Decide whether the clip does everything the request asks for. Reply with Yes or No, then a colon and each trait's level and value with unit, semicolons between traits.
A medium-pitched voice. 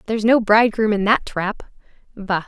No: high, 210 Hz